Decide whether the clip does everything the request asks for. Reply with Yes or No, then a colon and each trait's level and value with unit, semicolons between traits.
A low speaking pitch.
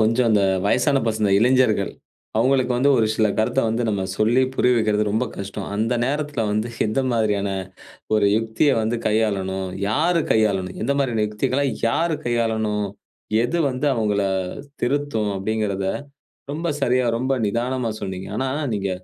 Yes: low, 110 Hz